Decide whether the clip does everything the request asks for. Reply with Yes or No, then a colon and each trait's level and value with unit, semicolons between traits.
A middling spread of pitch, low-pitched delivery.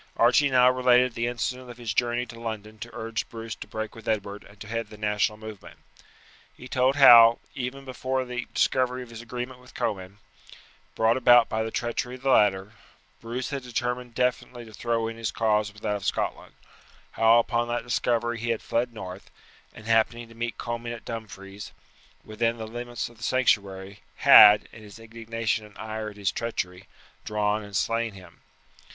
No: narrow, 2.2 semitones; low, 115 Hz